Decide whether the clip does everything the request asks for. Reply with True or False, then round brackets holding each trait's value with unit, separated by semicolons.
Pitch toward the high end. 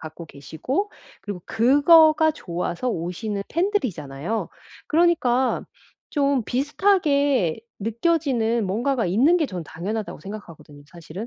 True (230 Hz)